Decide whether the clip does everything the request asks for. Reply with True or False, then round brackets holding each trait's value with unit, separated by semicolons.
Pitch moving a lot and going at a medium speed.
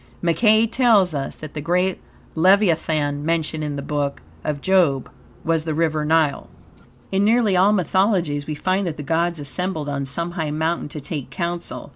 False (3.9 semitones; 170 wpm)